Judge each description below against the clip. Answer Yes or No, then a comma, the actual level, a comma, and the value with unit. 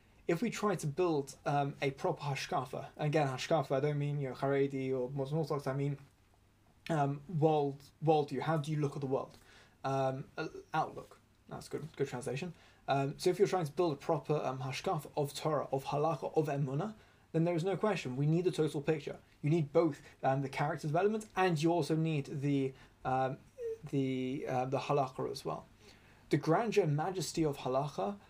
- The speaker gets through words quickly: No, average, 195 wpm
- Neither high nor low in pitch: Yes, medium, 145 Hz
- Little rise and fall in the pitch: No, average, 3.4 semitones